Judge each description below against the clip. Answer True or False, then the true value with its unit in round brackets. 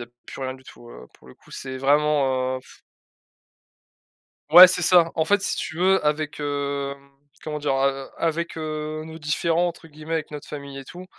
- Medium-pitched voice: True (150 Hz)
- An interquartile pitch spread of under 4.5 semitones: True (3.0 semitones)